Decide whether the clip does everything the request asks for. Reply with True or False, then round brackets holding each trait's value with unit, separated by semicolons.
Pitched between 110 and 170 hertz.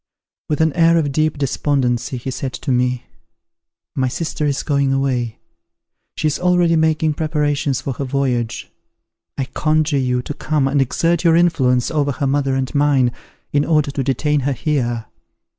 True (140 Hz)